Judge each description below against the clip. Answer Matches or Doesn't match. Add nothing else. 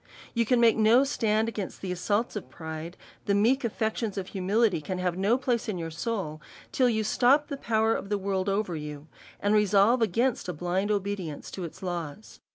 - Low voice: Doesn't match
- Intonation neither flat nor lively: Matches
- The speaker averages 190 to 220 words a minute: Matches